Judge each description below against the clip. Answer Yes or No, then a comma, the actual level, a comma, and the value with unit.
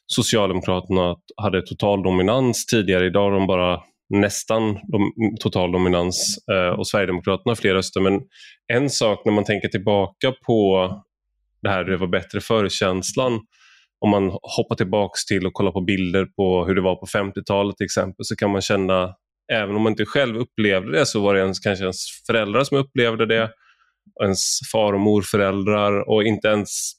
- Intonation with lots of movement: No, average, 2.7 semitones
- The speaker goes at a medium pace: Yes, average, 165 wpm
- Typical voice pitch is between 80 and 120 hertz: Yes, low, 100 Hz